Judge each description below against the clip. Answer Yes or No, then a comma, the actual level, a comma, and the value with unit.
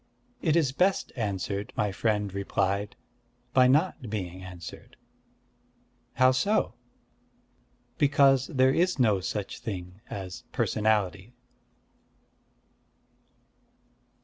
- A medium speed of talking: No, slow, 90 wpm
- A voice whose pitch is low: Yes, low, 110 Hz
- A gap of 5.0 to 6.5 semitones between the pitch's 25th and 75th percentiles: Yes, average, 5.3 semitones